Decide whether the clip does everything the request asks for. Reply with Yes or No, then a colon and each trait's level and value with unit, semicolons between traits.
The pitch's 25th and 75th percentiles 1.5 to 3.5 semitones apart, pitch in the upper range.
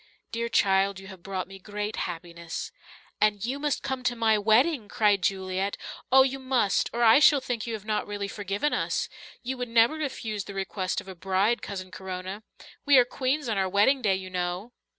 No: average, 4.2 semitones; high, 210 Hz